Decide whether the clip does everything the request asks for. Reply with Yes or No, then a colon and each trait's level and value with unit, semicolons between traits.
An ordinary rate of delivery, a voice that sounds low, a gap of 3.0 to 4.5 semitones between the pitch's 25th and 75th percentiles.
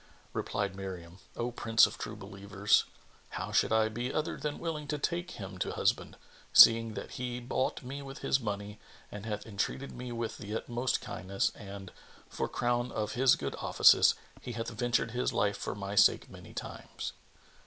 Yes: average, 175 wpm; low, 115 Hz; average, 3.5 semitones